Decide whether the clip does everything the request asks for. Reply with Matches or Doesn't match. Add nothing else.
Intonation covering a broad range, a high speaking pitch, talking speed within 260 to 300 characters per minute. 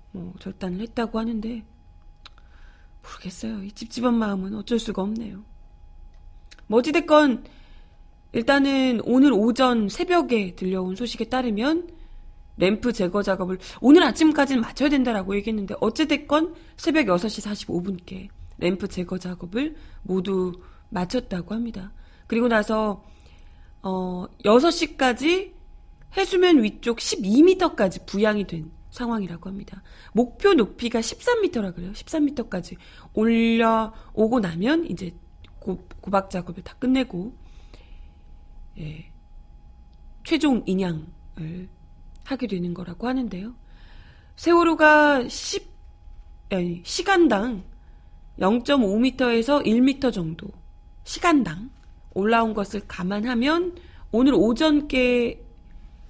Doesn't match